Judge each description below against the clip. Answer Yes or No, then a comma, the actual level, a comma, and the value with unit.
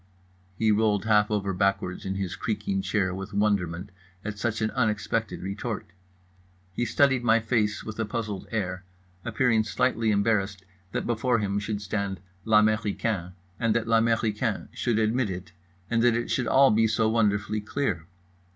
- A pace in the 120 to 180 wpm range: Yes, average, 160 wpm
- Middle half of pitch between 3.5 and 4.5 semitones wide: No, narrow, 2.4 semitones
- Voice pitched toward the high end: No, low, 105 Hz